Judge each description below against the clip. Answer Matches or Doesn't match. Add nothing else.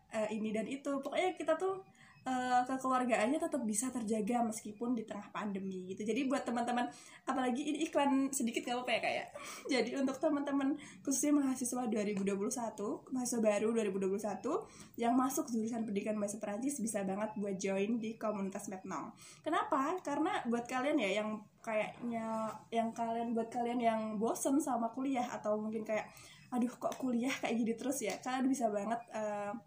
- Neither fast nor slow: Doesn't match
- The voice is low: Doesn't match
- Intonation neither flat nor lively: Matches